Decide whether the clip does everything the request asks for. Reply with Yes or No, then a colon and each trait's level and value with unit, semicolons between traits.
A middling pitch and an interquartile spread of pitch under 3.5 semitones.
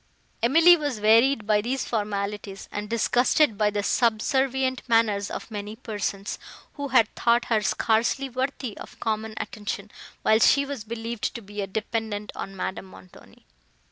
No: high, 220 Hz; average, 3.1 semitones